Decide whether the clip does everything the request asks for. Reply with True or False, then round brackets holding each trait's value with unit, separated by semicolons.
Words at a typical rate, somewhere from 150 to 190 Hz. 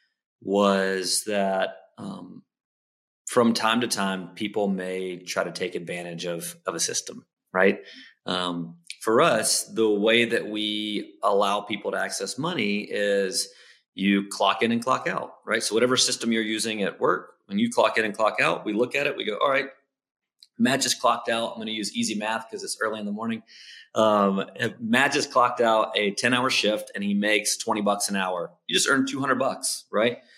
False (195 wpm; 105 Hz)